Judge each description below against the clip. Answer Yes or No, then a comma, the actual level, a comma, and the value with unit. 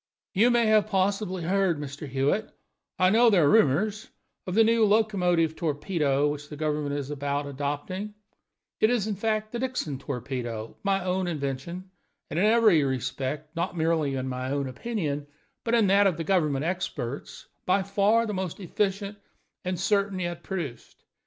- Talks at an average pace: Yes, average, 165 wpm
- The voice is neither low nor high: Yes, medium, 175 Hz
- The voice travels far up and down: Yes, wide, 6.0 semitones